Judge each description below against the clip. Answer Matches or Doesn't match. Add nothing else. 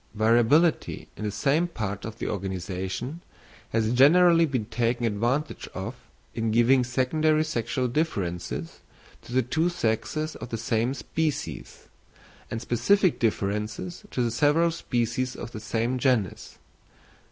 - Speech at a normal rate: Doesn't match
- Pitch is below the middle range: Matches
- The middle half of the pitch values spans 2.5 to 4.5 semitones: Doesn't match